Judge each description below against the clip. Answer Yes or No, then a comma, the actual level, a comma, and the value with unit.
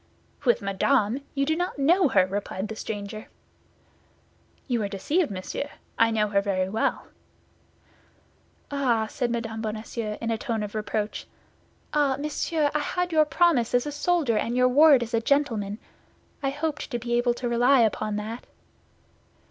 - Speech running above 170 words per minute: No, average, 160 wpm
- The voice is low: No, high, 235 Hz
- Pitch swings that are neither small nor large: Yes, average, 4.9 semitones